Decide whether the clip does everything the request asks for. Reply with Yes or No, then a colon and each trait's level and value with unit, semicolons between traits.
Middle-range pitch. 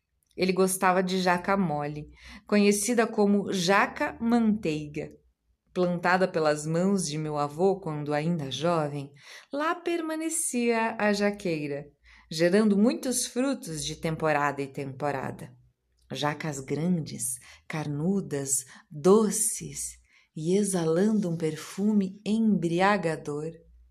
Yes: medium, 175 Hz